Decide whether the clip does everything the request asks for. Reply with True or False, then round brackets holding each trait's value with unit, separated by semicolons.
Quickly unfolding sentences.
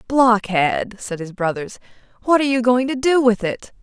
False (190 wpm)